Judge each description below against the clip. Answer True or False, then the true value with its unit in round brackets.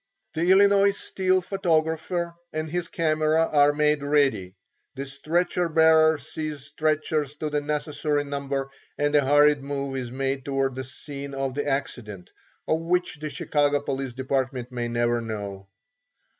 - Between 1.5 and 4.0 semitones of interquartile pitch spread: True (2.7 semitones)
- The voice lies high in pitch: False (145 Hz)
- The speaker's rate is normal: True (145 wpm)